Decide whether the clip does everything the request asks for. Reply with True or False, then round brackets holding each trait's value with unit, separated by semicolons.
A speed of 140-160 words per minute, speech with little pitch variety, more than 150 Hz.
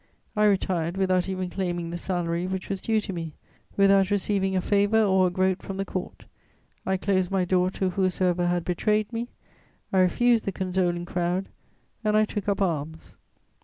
False (180 wpm; 1.9 semitones; 190 Hz)